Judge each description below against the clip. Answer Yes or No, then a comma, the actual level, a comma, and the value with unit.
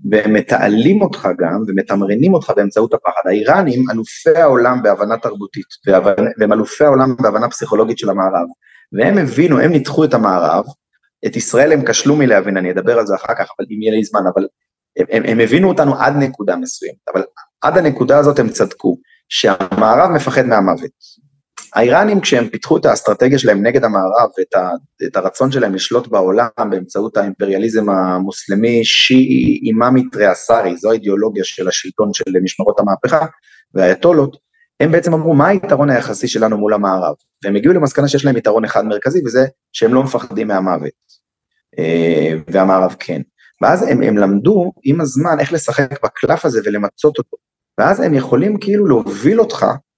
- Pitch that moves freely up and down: Yes, wide, 7.7 semitones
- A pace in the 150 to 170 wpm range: Yes, average, 160 wpm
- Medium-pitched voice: No, low, 125 Hz